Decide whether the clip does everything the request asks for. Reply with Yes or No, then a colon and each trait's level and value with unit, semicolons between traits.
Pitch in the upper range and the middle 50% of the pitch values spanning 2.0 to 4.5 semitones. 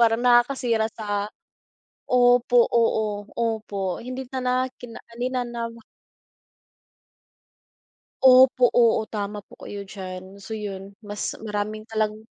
Yes: high, 220 Hz; average, 2.9 semitones